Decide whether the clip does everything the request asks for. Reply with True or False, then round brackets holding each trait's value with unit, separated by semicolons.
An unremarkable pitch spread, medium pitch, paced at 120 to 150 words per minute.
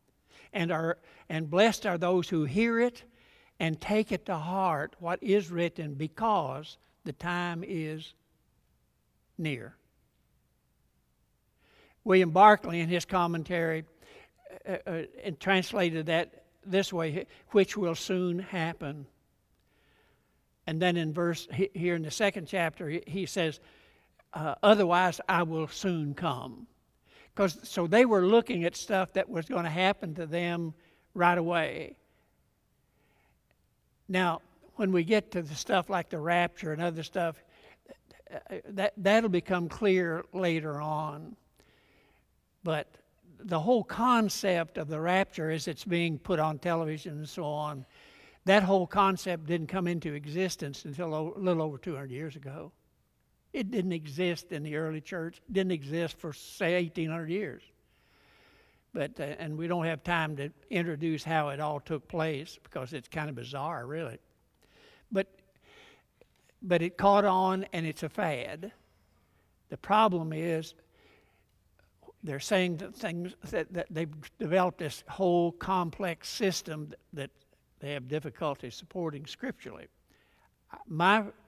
True (3.2 semitones; 170 Hz; 135 wpm)